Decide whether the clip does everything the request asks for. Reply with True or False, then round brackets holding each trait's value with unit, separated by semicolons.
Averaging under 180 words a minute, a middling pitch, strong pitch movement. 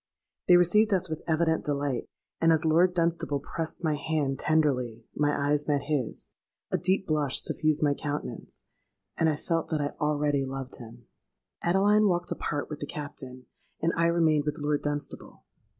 False (160 wpm; 150 Hz; 2.5 semitones)